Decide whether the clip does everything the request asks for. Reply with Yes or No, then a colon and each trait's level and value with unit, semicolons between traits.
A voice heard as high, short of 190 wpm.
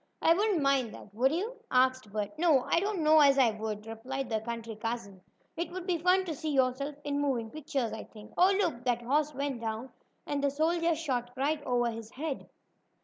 No: very high, 270 Hz; fast, 205 wpm